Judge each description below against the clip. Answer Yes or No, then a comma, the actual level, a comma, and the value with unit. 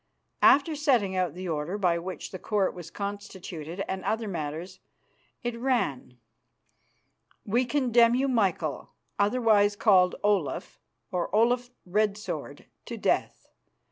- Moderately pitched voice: No, high, 200 Hz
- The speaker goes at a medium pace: No, slow, 125 wpm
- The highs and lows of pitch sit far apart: No, average, 4.5 semitones